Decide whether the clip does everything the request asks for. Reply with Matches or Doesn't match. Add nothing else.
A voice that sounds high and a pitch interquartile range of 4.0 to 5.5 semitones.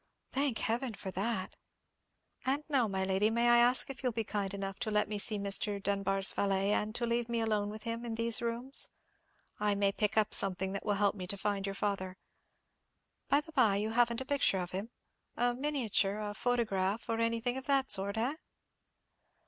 Doesn't match